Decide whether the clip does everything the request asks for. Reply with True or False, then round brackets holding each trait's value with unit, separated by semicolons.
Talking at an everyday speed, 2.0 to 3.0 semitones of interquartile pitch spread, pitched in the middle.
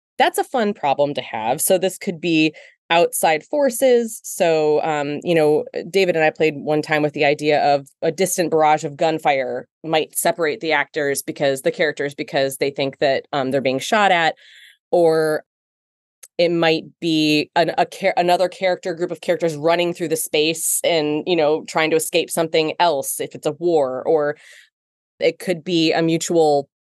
True (180 wpm; 2.7 semitones; 160 Hz)